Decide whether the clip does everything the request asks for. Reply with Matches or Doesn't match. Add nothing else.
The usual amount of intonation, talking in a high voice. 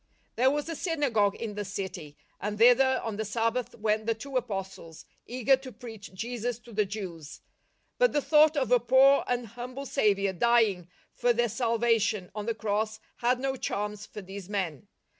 Matches